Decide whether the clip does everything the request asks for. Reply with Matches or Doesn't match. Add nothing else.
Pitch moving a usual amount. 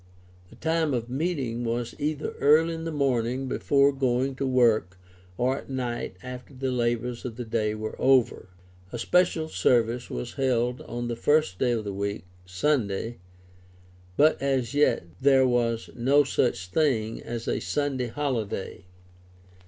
Matches